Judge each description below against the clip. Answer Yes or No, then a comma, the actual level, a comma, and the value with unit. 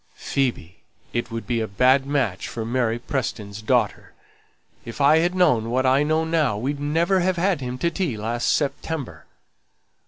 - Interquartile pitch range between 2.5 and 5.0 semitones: No, wide, 5.4 semitones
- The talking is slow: No, average, 165 wpm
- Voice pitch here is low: Yes, low, 130 Hz